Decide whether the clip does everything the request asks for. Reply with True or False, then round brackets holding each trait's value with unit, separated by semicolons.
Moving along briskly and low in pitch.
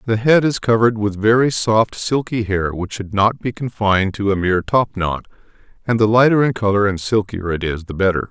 True (210 wpm; 105 Hz)